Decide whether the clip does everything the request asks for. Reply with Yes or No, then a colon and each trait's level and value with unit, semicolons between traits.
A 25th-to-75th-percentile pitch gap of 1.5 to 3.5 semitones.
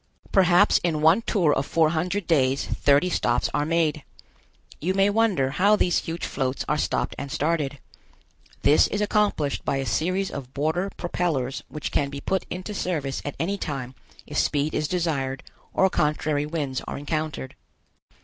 No: average, 4.4 semitones